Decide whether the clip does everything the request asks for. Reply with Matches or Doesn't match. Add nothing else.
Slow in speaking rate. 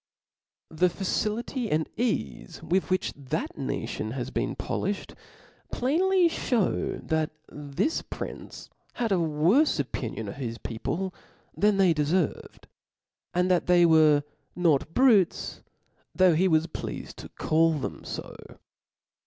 Matches